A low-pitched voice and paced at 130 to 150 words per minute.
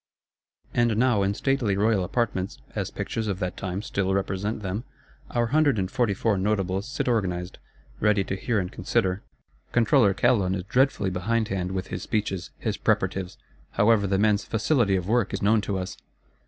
No: low, 100 Hz; average, 170 wpm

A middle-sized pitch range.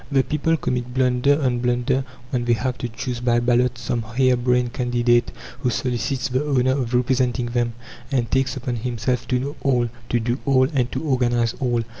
No: narrow, 1.4 semitones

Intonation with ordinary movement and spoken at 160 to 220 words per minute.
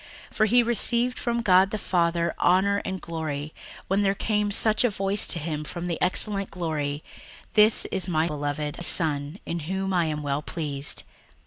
Yes: average, 4.7 semitones; average, 180 wpm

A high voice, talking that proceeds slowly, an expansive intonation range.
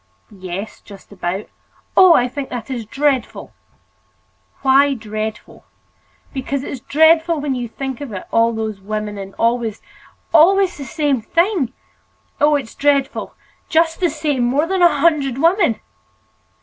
Yes: very high, 270 Hz; slow, 125 wpm; wide, 5.8 semitones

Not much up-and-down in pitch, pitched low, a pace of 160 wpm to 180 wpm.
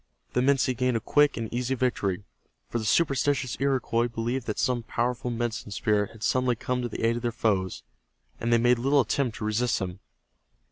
No: narrow, 2.3 semitones; low, 120 Hz; average, 195 wpm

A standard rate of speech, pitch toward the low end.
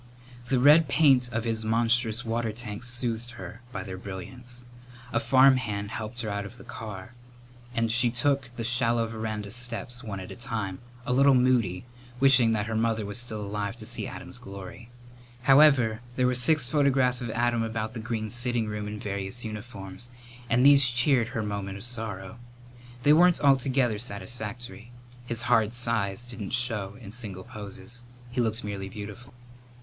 Yes: average, 170 wpm; low, 115 Hz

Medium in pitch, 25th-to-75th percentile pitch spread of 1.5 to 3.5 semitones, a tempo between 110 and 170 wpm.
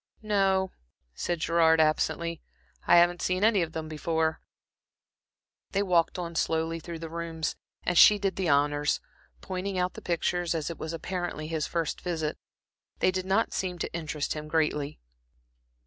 Yes: medium, 170 Hz; narrow, 2.4 semitones; average, 160 wpm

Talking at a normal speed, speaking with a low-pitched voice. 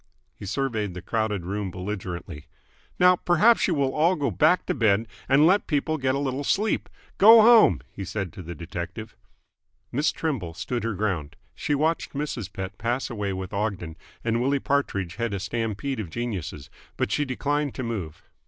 Yes: average, 180 wpm; low, 115 Hz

